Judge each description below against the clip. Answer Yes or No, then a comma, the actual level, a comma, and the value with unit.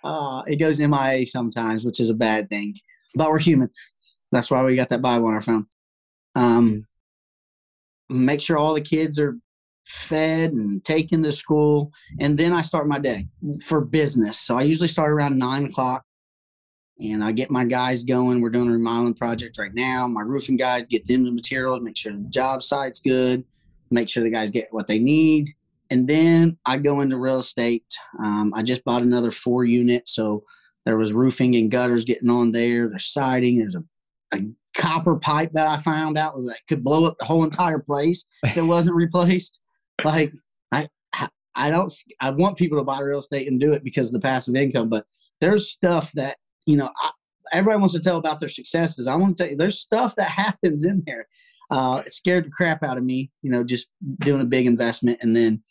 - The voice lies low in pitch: Yes, low, 130 Hz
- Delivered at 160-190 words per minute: No, fast, 205 wpm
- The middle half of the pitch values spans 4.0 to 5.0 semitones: Yes, average, 4.7 semitones